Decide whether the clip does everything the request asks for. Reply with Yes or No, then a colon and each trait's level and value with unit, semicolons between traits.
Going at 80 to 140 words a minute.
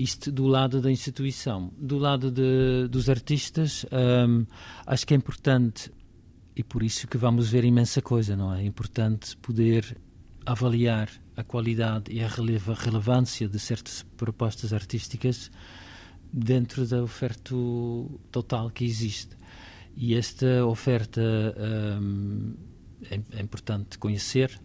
Yes: average, 130 wpm